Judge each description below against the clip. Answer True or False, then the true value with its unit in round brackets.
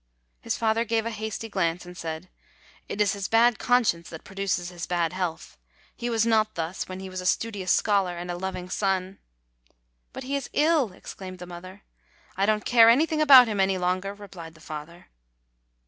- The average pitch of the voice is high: True (195 Hz)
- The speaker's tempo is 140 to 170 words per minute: False (195 wpm)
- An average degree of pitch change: True (4.0 semitones)